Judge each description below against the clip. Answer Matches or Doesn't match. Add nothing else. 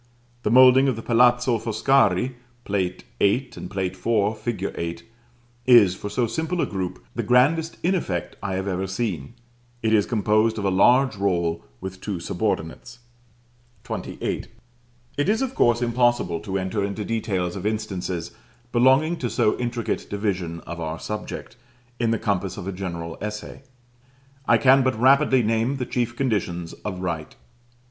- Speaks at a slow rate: Doesn't match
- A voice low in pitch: Matches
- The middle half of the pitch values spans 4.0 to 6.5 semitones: Matches